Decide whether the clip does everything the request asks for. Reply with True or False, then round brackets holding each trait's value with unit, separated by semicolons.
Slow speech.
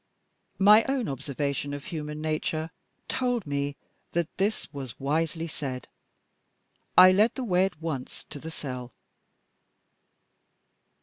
True (120 wpm)